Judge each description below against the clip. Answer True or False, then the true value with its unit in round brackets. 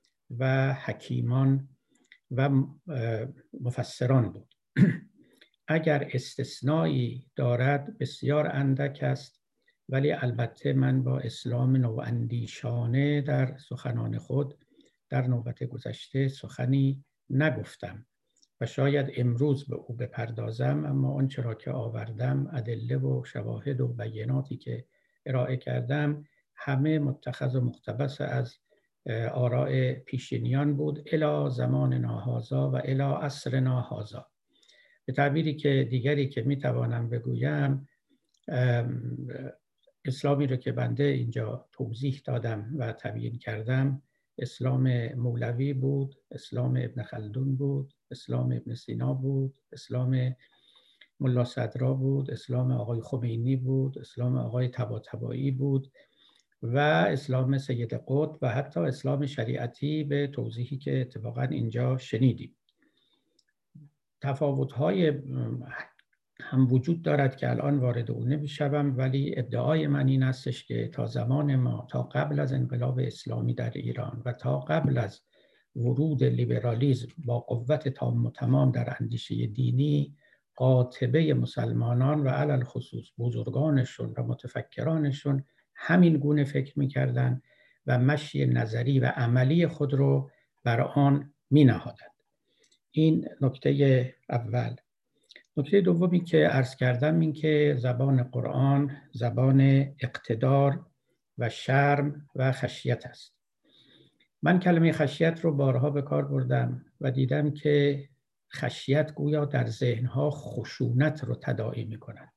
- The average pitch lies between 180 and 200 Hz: False (130 Hz)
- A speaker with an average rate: True (115 wpm)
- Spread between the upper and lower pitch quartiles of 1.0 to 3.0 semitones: True (2.5 semitones)